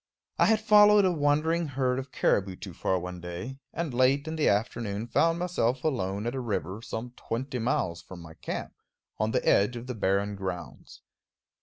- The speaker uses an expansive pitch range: Yes, wide, 6.7 semitones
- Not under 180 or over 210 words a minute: Yes, average, 185 wpm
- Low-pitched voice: Yes, low, 120 Hz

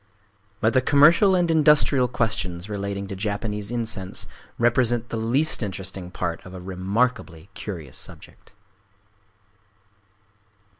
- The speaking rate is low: Yes, slow, 110 wpm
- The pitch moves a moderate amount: Yes, average, 4.7 semitones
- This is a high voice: No, low, 110 Hz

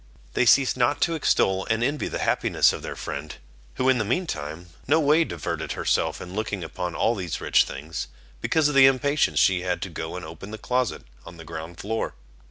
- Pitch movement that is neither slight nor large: No, wide, 7.5 semitones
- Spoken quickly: Yes, fast, 210 wpm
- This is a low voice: Yes, low, 110 Hz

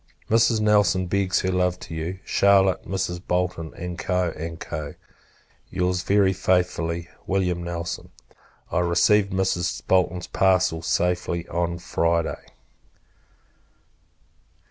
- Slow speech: Yes, slow, 100 wpm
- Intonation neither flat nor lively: No, narrow, 1.7 semitones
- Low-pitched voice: Yes, very low, 90 Hz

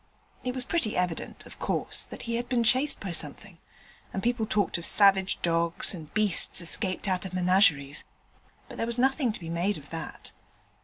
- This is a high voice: Yes, high, 195 Hz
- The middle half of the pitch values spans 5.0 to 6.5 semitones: Yes, wide, 5.4 semitones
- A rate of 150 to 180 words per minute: No, average, 190 wpm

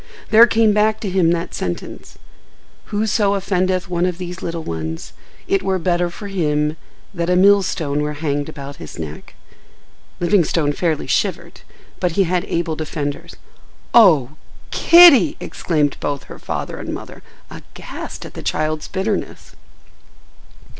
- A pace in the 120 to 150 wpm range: Yes, average, 140 wpm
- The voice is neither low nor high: Yes, medium, 175 Hz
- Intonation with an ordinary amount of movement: Yes, average, 4.5 semitones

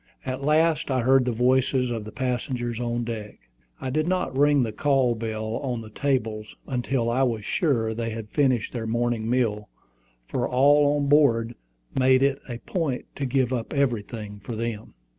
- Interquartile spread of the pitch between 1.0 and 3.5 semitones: Yes, average, 3.1 semitones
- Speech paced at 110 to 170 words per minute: No, average, 180 wpm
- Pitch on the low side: Yes, low, 125 Hz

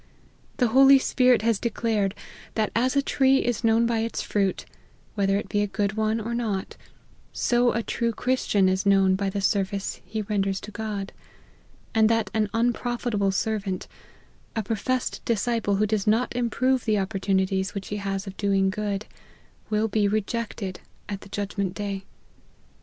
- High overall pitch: Yes, high, 210 Hz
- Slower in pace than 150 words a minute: No, average, 165 wpm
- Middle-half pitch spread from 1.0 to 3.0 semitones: Yes, average, 2.7 semitones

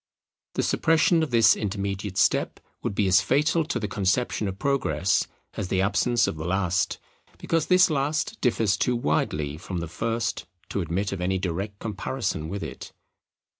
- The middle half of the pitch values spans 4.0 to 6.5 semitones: Yes, average, 4.9 semitones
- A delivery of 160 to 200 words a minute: Yes, average, 170 wpm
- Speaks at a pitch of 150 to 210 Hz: No, low, 100 Hz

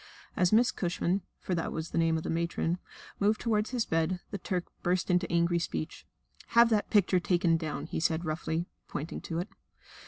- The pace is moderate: Yes, average, 190 wpm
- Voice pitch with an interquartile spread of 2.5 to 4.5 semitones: Yes, average, 2.9 semitones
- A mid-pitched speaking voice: Yes, medium, 175 Hz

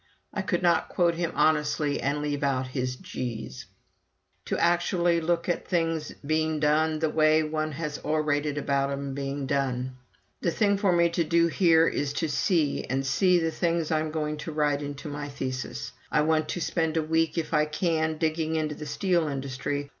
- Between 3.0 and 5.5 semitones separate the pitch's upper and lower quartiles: No, narrow, 2.6 semitones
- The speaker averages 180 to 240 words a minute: Yes, average, 185 wpm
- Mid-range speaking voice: Yes, medium, 155 Hz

